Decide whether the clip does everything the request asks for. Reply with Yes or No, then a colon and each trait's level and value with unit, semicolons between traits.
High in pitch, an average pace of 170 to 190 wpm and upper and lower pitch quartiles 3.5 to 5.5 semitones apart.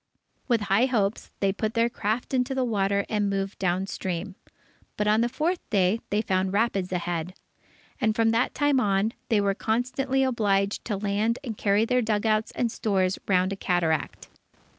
No: high, 210 Hz; average, 175 wpm; average, 3.1 semitones